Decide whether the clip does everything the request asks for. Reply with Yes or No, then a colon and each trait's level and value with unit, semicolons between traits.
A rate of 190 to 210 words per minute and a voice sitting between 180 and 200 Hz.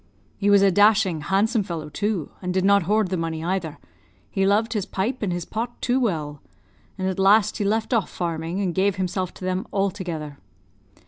Yes: average, 195 wpm; high, 190 Hz